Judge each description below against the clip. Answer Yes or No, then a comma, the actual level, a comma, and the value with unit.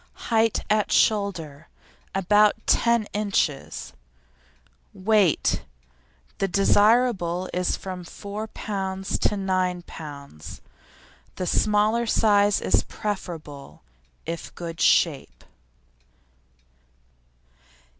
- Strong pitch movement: No, average, 3.8 semitones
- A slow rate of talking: Yes, slow, 85 wpm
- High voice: Yes, high, 195 Hz